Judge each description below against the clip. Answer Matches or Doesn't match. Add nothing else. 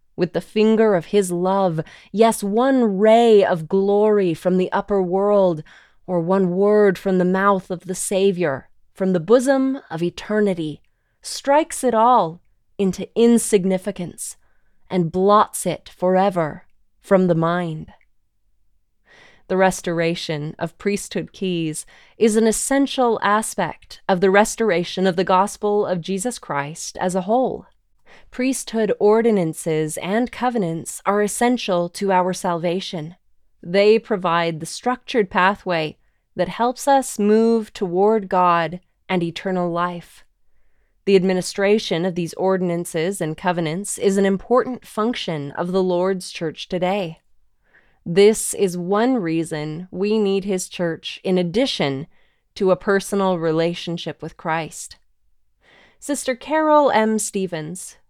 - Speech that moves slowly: Matches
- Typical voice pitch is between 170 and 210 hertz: Matches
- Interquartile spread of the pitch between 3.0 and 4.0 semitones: Matches